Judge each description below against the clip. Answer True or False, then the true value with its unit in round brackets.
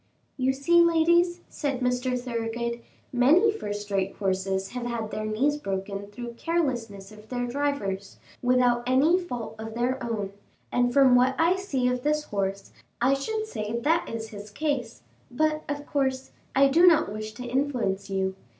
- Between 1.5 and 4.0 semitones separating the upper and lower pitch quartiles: False (5.0 semitones)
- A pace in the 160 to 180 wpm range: True (170 wpm)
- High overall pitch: True (245 Hz)